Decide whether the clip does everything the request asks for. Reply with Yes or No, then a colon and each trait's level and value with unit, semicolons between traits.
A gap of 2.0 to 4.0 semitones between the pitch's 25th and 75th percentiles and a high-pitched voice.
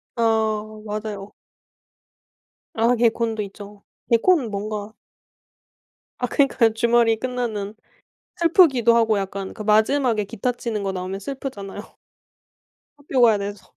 Yes: average, 3.0 semitones; high, 220 Hz